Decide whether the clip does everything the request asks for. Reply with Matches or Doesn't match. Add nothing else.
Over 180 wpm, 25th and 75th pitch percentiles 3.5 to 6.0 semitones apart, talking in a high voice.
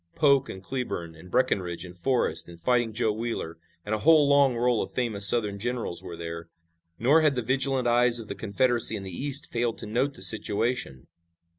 Doesn't match